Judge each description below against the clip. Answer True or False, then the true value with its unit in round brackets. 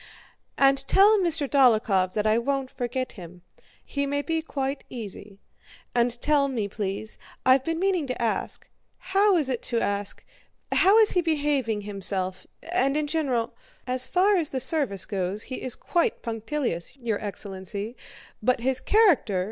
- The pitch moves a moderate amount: False (5.8 semitones)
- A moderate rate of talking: False (130 wpm)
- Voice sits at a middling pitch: False (255 Hz)